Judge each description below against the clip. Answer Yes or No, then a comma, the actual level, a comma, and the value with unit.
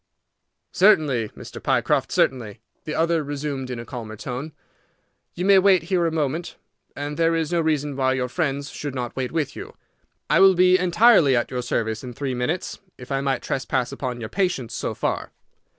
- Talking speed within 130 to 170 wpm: No, average, 185 wpm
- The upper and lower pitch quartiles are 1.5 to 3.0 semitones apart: No, average, 4.7 semitones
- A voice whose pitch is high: No, medium, 140 Hz